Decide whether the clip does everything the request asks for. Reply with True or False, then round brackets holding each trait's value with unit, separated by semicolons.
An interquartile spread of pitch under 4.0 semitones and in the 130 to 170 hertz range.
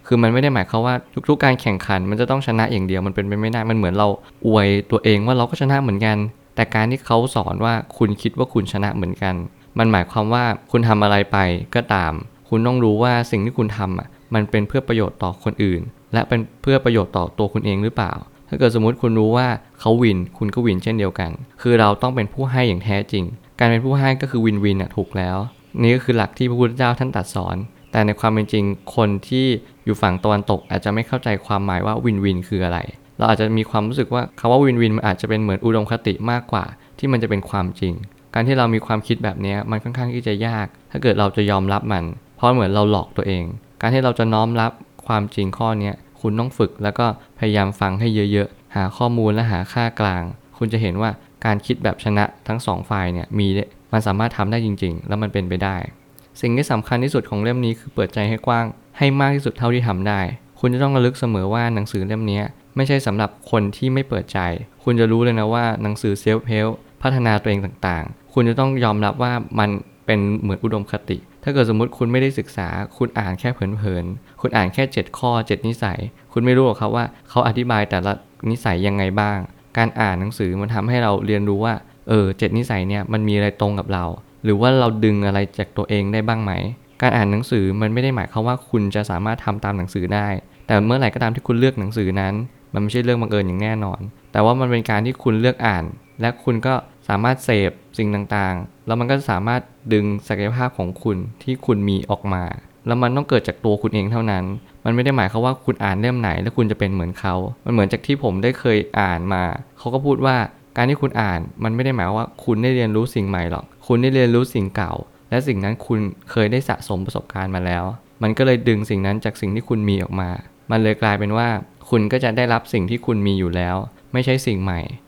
False (3.3 semitones; 110 Hz)